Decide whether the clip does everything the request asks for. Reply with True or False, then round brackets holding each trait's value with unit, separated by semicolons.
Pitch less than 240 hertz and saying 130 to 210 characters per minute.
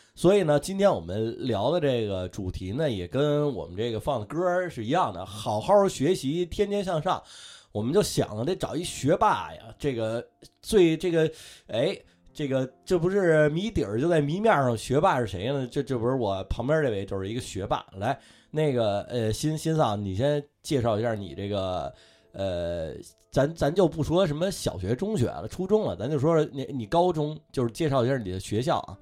False (140 Hz; 280 characters per minute)